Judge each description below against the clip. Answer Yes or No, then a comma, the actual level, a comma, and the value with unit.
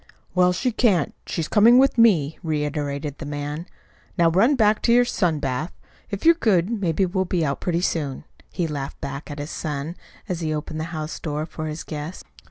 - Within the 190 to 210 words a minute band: Yes, average, 195 wpm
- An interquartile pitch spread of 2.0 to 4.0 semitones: No, average, 4.4 semitones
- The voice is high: No, medium, 165 Hz